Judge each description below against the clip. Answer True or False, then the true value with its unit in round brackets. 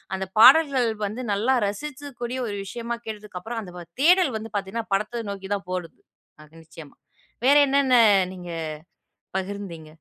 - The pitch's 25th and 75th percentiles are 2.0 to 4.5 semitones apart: False (4.9 semitones)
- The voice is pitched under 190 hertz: False (215 Hz)